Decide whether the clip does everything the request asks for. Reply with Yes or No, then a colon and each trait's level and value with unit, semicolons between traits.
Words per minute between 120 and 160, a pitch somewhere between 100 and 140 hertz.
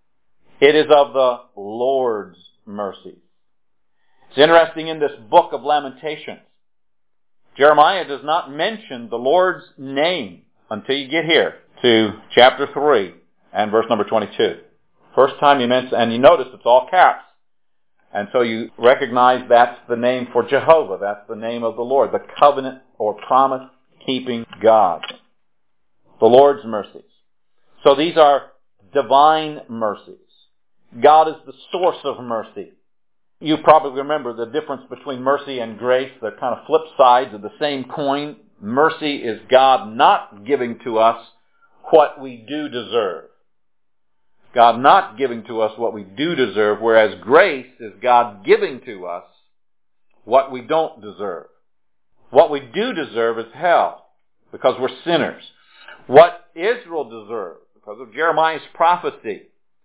Yes: average, 140 wpm; low, 135 Hz